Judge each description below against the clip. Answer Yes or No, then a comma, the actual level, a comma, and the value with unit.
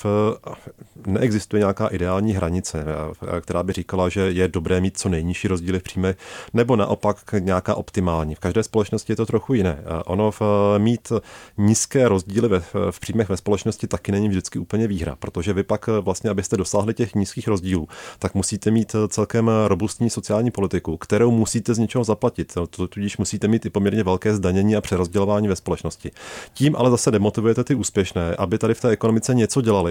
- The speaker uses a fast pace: Yes, fast, 175 wpm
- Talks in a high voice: No, low, 105 Hz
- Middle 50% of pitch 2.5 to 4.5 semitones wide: Yes, average, 2.9 semitones